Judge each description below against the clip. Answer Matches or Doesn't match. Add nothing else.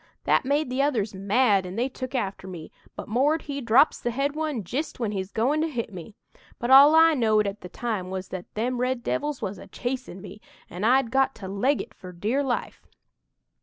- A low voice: Doesn't match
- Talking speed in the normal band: Doesn't match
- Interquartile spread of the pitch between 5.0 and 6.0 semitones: Matches